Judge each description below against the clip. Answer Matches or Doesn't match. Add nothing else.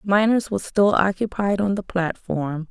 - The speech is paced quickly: Doesn't match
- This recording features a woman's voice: Matches